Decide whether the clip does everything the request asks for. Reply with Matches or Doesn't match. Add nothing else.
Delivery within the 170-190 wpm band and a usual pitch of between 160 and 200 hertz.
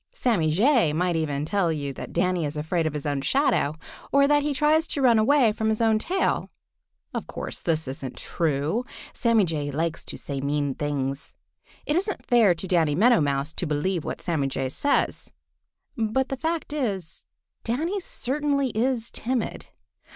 Matches